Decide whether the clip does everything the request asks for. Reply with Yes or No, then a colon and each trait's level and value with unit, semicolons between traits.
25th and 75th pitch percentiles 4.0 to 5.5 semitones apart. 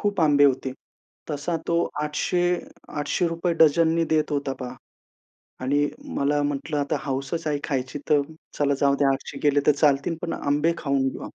No: narrow, 2.5 semitones